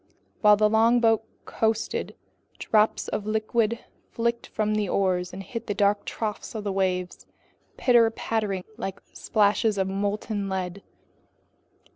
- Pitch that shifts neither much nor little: No, narrow, 2.2 semitones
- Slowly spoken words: Yes, slow, 130 wpm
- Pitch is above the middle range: Yes, high, 210 Hz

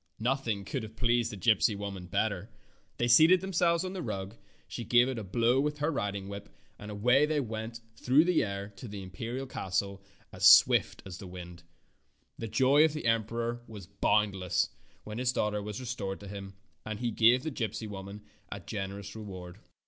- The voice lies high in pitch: No, low, 110 Hz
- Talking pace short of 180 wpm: No, average, 185 wpm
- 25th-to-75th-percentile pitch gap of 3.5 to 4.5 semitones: Yes, average, 3.9 semitones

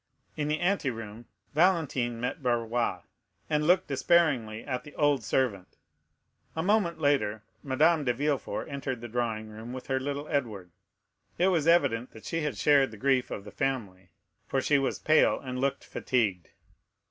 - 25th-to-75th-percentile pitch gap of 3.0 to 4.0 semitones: No, average, 4.7 semitones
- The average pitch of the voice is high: No, low, 130 Hz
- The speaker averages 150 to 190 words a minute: Yes, average, 160 wpm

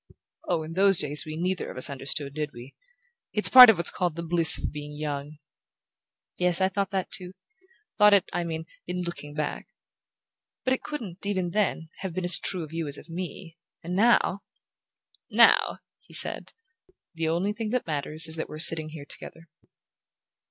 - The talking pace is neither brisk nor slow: Yes, average, 185 wpm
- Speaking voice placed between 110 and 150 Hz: No, medium, 170 Hz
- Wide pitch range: No, average, 3.5 semitones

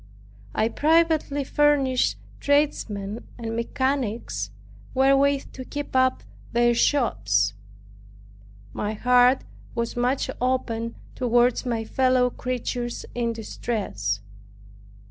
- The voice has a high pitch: Yes, high, 245 Hz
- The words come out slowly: Yes, slow, 90 wpm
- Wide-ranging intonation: No, average, 2.8 semitones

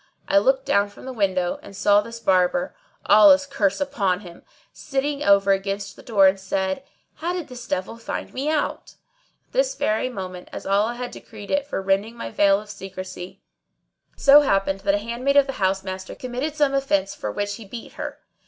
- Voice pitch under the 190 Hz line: No, high, 205 Hz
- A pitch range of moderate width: No, wide, 5.9 semitones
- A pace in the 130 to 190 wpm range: No, average, 200 wpm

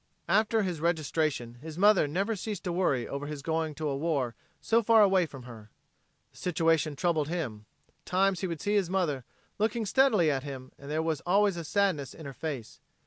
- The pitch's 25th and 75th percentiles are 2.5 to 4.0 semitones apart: No, average, 5.1 semitones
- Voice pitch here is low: No, medium, 165 Hz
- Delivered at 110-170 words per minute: No, fast, 205 wpm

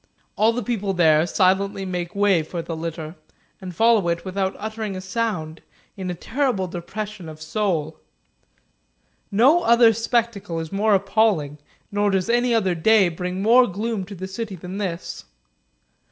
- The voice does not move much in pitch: No, average, 4.0 semitones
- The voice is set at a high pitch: Yes, high, 195 Hz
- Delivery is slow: No, average, 155 wpm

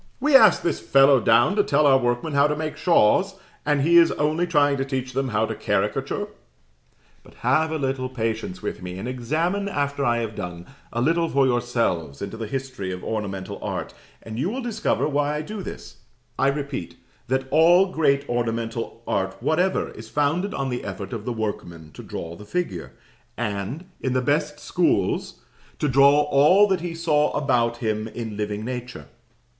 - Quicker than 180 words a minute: Yes, average, 190 wpm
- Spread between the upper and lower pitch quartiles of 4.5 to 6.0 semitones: Yes, wide, 5.4 semitones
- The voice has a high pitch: No, low, 135 Hz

